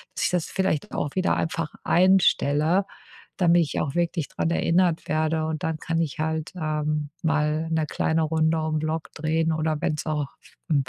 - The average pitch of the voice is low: No, medium, 160 Hz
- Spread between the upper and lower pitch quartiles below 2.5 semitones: Yes, narrow, 1.3 semitones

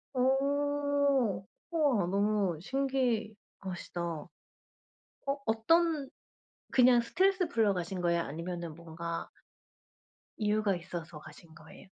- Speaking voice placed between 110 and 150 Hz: No, high, 195 Hz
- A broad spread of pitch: Yes, wide, 6.4 semitones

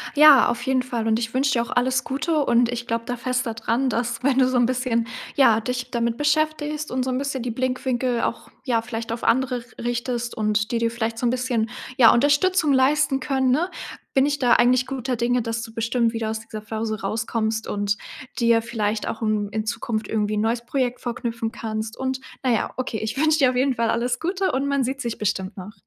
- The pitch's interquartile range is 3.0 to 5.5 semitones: No, narrow, 2.5 semitones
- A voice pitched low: No, high, 240 Hz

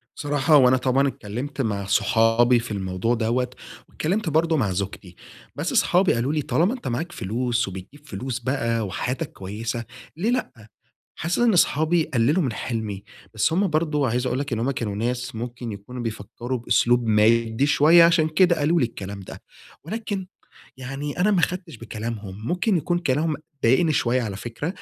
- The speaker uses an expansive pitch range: Yes, wide, 5.7 semitones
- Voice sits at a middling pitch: No, low, 125 Hz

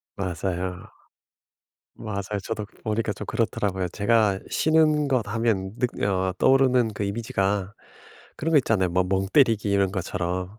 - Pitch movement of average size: Yes, average, 3.5 semitones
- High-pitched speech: No, low, 105 Hz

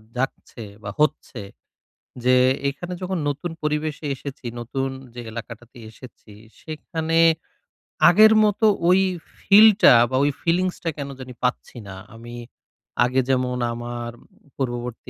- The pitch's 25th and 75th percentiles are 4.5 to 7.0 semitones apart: Yes, average, 5.1 semitones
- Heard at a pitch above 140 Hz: No, low, 135 Hz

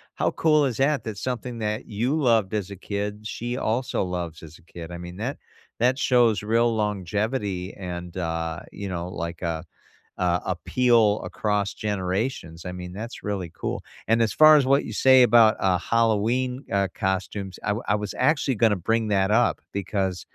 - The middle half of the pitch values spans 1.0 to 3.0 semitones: No, average, 4.4 semitones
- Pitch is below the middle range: Yes, low, 105 Hz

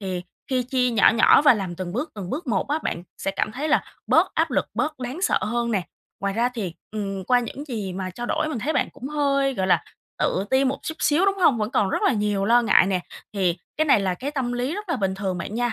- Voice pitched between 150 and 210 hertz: No, high, 235 Hz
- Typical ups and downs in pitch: No, wide, 5.9 semitones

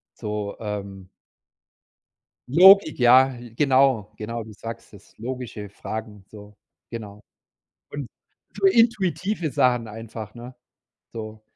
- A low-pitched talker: Yes, low, 115 Hz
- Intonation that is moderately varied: Yes, average, 3.9 semitones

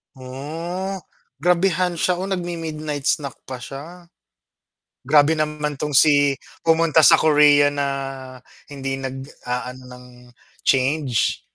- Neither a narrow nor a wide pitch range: Yes, average, 3.5 semitones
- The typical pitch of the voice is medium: Yes, medium, 150 Hz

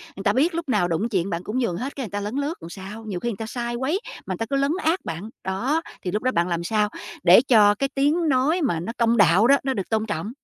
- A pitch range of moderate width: No, wide, 5.8 semitones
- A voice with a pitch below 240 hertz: Yes, high, 225 Hz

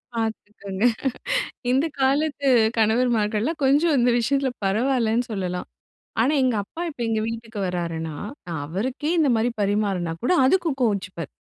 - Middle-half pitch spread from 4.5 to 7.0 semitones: Yes, average, 5.1 semitones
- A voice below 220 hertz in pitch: No, high, 225 Hz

